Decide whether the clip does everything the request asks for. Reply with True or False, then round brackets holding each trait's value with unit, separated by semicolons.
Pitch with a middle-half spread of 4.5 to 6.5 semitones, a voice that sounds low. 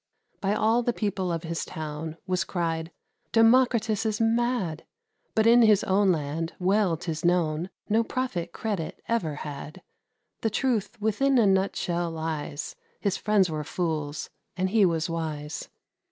False (5.2 semitones; 185 Hz)